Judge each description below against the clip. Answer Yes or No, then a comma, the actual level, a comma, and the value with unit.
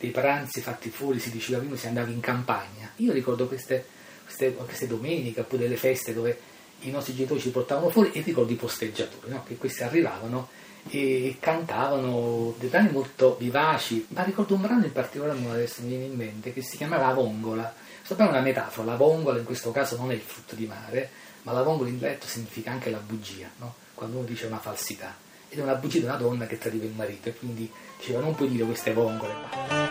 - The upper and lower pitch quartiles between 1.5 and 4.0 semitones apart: Yes, average, 2.7 semitones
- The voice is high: No, low, 125 Hz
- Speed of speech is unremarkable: No, fast, 215 wpm